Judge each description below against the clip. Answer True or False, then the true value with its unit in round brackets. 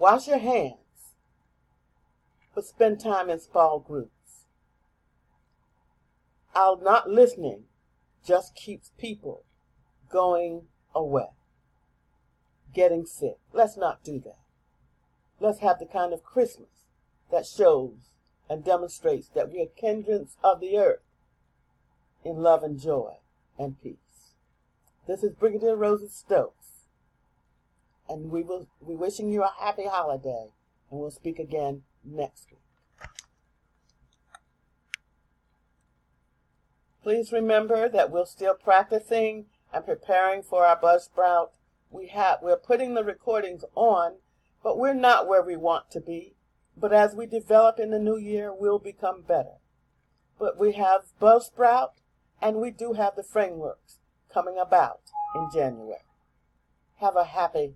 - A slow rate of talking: True (125 wpm)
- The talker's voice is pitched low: False (195 Hz)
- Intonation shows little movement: False (4.8 semitones)